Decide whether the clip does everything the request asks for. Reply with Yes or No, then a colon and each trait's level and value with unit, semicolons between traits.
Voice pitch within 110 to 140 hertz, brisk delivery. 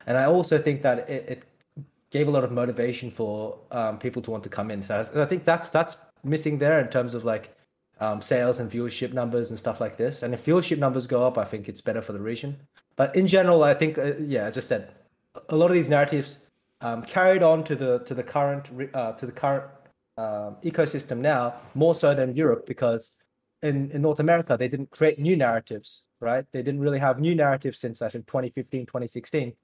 Yes: low, 135 Hz; fast, 220 wpm